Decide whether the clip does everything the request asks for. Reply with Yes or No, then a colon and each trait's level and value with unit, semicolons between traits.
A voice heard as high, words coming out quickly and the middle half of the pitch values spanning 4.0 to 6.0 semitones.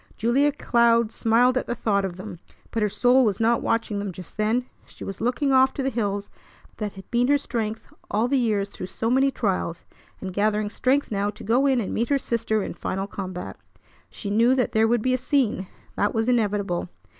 No: high, 225 Hz; fast, 215 wpm; average, 3.5 semitones